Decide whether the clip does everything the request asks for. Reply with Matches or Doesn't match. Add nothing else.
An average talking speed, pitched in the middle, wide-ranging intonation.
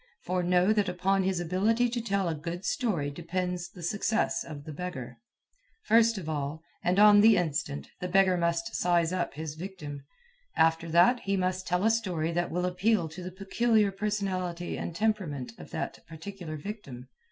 Doesn't match